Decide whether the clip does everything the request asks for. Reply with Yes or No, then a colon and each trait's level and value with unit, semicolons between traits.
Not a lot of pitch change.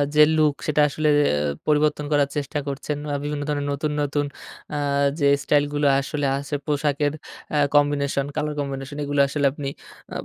Yes: narrow, 0.9 semitones